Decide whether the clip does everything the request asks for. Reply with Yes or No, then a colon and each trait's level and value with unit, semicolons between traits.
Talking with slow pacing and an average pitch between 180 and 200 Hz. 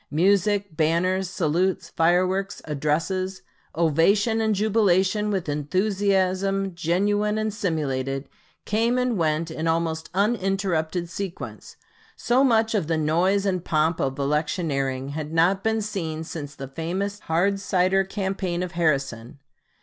Yes: slow, 125 wpm; medium, 185 Hz